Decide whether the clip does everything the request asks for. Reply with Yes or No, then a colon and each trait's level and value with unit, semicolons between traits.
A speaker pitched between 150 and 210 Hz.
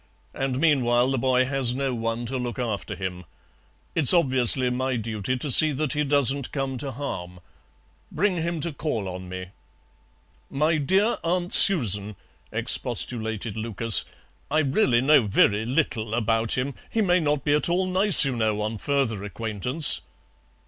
No: low, 130 Hz